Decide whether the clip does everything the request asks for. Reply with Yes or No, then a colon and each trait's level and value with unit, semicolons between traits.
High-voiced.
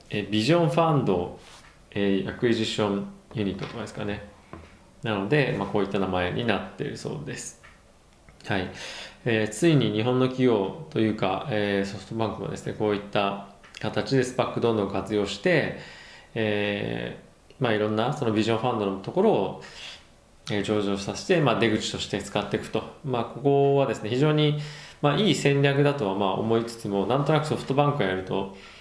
No: low, 110 Hz